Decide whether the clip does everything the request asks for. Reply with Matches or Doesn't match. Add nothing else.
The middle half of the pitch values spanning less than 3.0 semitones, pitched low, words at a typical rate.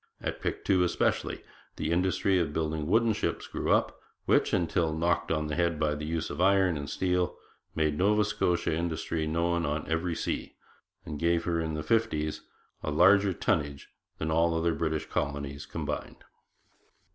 Matches